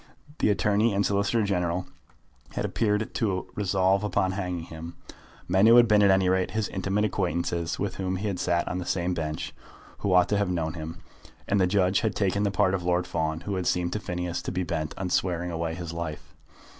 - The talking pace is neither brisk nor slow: No, fast, 220 wpm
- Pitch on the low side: Yes, very low, 95 Hz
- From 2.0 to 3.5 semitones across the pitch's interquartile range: Yes, narrow, 2.6 semitones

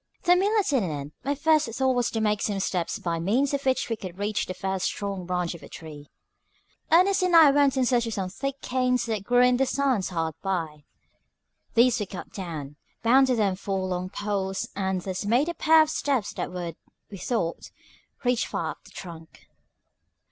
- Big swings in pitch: Yes, wide, 6.3 semitones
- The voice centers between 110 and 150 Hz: No, high, 210 Hz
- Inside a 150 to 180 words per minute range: No, fast, 205 wpm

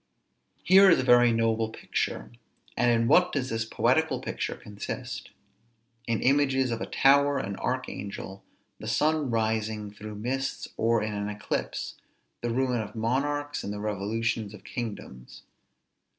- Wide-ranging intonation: No, average, 3.9 semitones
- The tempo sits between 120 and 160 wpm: Yes, average, 145 wpm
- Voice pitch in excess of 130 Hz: No, low, 115 Hz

